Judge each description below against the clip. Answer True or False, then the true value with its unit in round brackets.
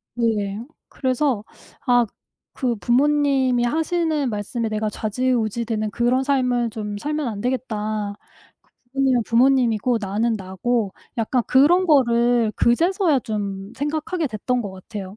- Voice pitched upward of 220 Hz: True (240 Hz)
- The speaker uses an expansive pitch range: False (3.7 semitones)